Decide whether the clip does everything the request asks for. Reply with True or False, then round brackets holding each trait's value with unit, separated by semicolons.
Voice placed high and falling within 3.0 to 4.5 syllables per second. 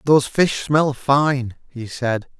False (130 Hz; 3.4 syllables/s)